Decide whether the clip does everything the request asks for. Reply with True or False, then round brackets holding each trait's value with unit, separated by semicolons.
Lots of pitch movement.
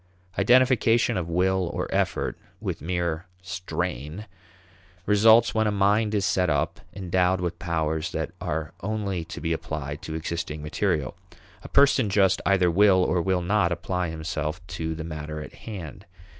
False (4.0 semitones)